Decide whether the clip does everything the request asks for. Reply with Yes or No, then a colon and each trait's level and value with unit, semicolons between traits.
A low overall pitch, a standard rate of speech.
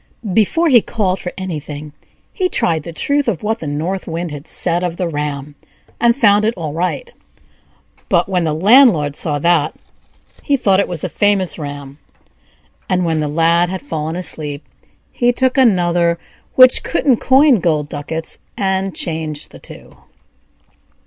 No: medium, 175 Hz; average, 160 wpm